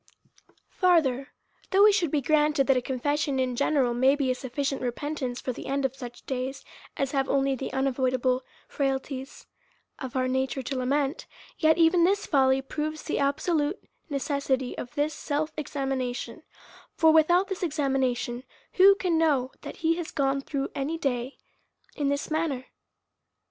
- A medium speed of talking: Yes, average, 160 wpm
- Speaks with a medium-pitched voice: No, very high, 275 Hz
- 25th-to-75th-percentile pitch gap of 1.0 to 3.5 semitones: Yes, average, 2.9 semitones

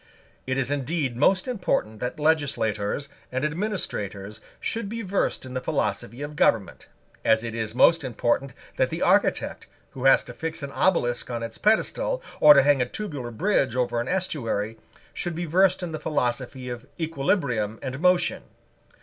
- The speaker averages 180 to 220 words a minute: No, average, 165 wpm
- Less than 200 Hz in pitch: Yes, low, 135 Hz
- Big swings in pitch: Yes, wide, 6.0 semitones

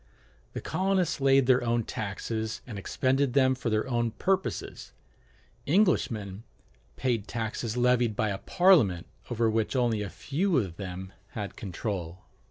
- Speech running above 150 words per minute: No, average, 140 wpm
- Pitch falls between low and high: No, low, 115 Hz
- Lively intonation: No, average, 4.4 semitones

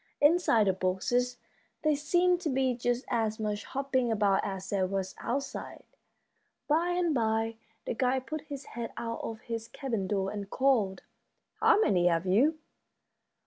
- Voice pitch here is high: Yes, high, 235 Hz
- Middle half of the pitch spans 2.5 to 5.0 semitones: No, wide, 5.4 semitones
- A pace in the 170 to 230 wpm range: No, average, 155 wpm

